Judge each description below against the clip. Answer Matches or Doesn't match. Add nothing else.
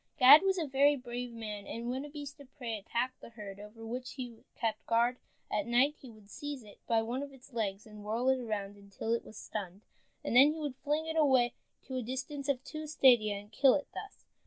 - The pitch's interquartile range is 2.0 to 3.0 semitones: Doesn't match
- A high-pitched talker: Matches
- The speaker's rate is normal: Doesn't match